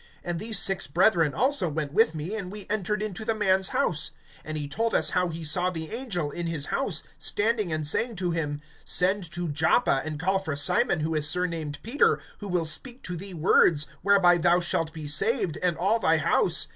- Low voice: No, medium, 175 Hz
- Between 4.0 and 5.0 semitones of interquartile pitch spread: Yes, average, 4.4 semitones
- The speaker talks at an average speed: No, fast, 210 wpm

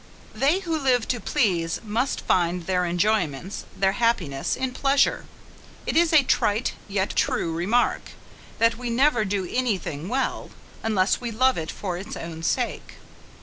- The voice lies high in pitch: Yes, high, 215 Hz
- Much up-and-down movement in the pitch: Yes, wide, 5.9 semitones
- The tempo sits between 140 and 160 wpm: Yes, average, 155 wpm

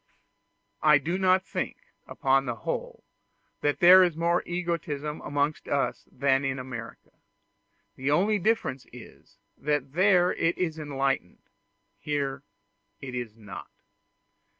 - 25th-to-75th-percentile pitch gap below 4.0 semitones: No, average, 4.3 semitones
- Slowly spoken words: Yes, slow, 125 wpm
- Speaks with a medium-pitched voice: Yes, medium, 145 Hz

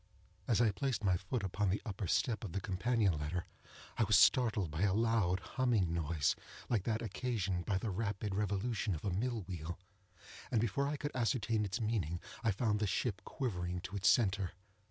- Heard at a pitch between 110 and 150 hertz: No, low, 100 Hz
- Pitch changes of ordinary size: Yes, average, 3.8 semitones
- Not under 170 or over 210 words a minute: Yes, average, 190 wpm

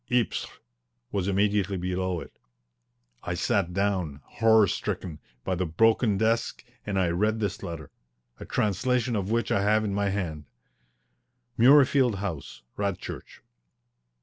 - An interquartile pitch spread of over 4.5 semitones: No, average, 3.4 semitones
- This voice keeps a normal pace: No, slow, 130 wpm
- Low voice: Yes, low, 100 Hz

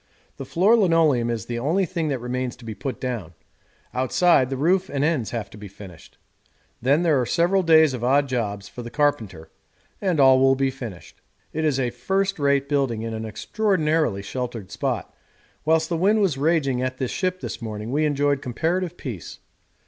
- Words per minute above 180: Yes, average, 190 wpm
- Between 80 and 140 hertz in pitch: Yes, low, 135 Hz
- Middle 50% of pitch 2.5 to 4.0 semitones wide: No, average, 5.3 semitones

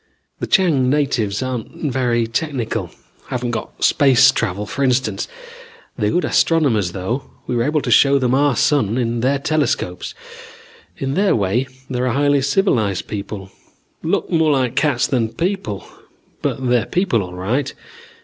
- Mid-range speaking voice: No, low, 130 Hz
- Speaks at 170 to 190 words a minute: No, average, 150 wpm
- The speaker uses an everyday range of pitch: Yes, average, 4.0 semitones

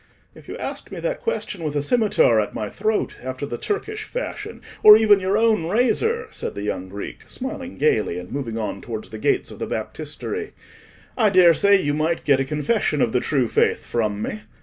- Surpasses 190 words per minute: Yes, average, 200 wpm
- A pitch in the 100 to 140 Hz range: No, medium, 155 Hz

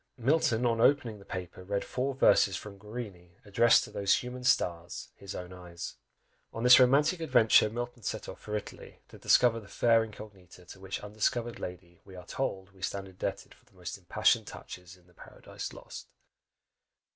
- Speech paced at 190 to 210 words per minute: No, average, 180 wpm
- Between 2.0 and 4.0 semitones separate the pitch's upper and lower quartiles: No, average, 4.6 semitones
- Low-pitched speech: Yes, low, 105 Hz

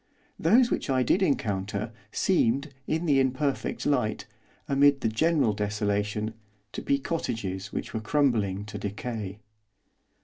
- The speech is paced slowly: Yes, slow, 130 wpm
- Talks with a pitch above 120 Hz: No, low, 115 Hz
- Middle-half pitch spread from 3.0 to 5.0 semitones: No, wide, 5.5 semitones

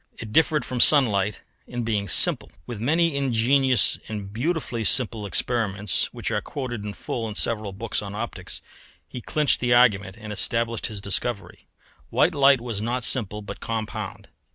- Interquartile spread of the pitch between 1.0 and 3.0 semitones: No, average, 3.4 semitones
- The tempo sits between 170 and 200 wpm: No, average, 160 wpm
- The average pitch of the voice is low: Yes, low, 115 Hz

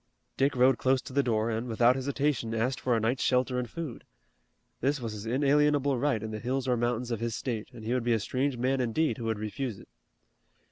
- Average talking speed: No, fast, 230 wpm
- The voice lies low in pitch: Yes, low, 125 Hz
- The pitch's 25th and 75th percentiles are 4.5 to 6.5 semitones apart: No, average, 2.9 semitones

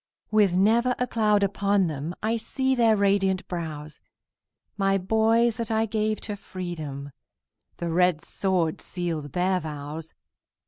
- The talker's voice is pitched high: Yes, high, 195 Hz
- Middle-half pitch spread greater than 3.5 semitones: Yes, average, 4.5 semitones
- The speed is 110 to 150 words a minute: Yes, slow, 135 wpm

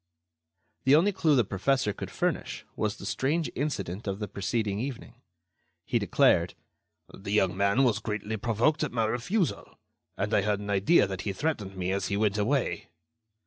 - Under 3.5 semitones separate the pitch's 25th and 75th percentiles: No, average, 5.3 semitones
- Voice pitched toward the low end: Yes, low, 105 Hz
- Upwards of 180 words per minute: No, average, 175 wpm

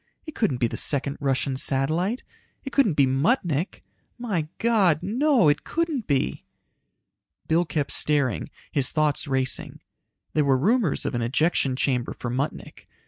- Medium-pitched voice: Yes, medium, 150 Hz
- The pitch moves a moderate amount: No, wide, 7.2 semitones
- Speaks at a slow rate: No, average, 145 wpm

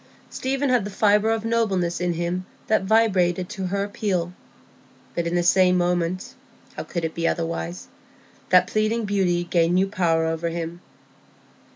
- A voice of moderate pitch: Yes, medium, 180 Hz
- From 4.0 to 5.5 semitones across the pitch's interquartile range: No, average, 3.1 semitones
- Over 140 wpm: Yes, average, 150 wpm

